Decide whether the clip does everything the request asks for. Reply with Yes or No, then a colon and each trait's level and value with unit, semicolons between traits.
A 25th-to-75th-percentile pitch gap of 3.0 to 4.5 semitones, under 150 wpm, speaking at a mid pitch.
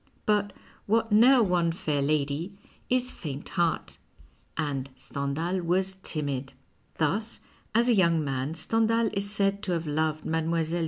No: average, 5.1 semitones; average, 140 wpm; medium, 170 Hz